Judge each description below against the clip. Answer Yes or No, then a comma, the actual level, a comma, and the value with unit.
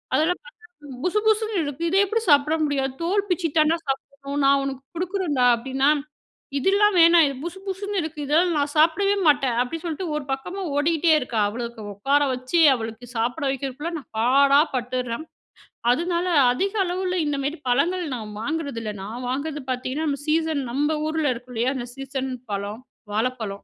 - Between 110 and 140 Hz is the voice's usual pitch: No, very high, 285 Hz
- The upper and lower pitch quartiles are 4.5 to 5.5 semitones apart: Yes, average, 4.9 semitones